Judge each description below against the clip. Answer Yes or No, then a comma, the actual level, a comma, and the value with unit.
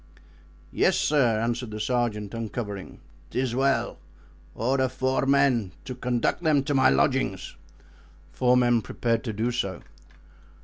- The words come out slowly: Yes, slow, 130 wpm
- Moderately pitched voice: No, low, 120 Hz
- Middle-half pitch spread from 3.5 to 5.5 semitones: No, average, 2.9 semitones